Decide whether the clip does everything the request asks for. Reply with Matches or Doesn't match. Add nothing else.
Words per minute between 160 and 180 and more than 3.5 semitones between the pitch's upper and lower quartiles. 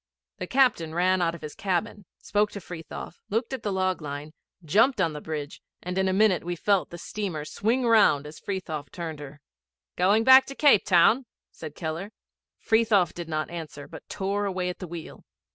Doesn't match